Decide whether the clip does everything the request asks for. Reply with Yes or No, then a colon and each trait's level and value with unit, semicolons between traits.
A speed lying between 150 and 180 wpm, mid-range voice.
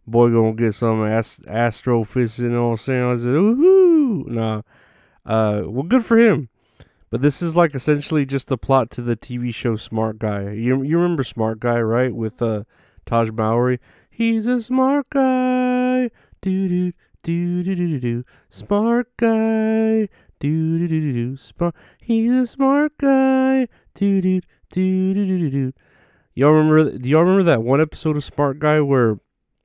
Yes: average, 160 wpm; medium, 145 Hz